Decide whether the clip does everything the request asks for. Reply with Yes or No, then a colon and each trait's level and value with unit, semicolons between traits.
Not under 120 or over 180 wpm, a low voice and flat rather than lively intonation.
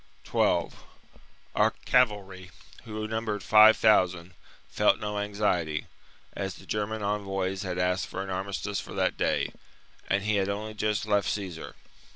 Yes: average, 140 wpm; low, 100 Hz; narrow, 2.2 semitones